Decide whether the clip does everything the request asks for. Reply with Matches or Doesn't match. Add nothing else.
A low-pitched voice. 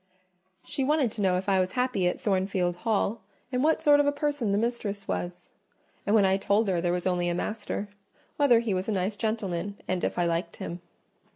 Doesn't match